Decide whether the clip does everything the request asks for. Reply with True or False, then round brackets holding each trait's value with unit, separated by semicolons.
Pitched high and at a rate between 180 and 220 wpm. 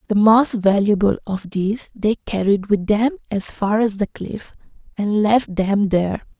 False (210 Hz; 170 wpm)